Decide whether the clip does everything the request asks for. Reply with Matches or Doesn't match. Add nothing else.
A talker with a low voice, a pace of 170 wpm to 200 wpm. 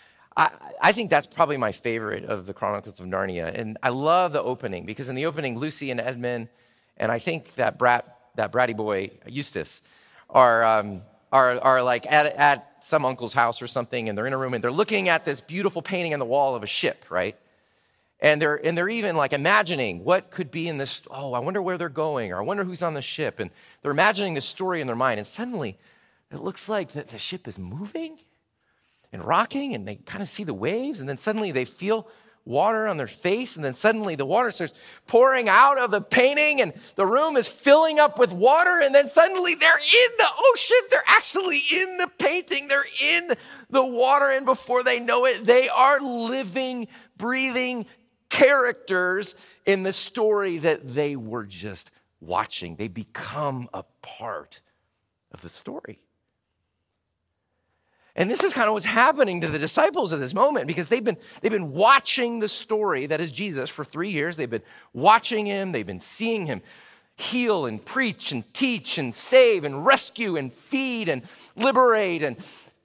Doesn't match